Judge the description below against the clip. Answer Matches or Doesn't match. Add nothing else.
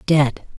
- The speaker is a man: Doesn't match